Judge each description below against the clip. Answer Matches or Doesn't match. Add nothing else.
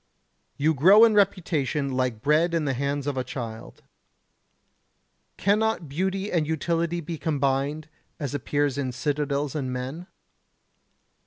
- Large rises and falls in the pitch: Doesn't match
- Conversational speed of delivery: Doesn't match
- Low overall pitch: Doesn't match